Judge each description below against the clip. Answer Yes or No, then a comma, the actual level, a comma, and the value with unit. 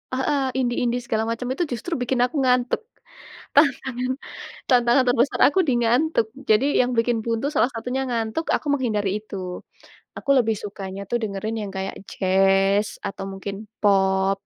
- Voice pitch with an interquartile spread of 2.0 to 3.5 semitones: No, average, 4.3 semitones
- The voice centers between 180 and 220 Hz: No, high, 235 Hz